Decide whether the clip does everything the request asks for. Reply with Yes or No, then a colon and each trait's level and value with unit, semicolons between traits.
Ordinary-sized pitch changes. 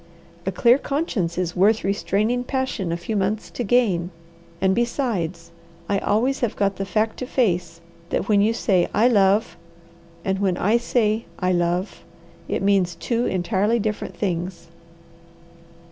Yes: average, 4.0 semitones